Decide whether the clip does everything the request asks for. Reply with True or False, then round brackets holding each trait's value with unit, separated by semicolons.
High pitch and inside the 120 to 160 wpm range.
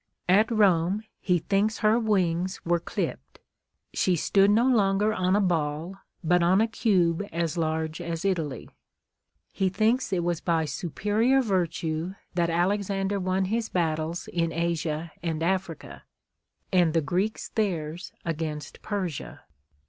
False (180 Hz; 135 wpm)